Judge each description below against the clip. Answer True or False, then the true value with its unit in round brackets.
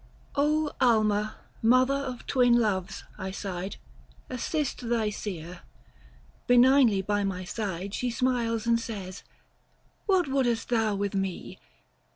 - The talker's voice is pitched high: True (225 Hz)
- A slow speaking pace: True (120 wpm)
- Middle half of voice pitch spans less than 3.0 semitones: False (4.1 semitones)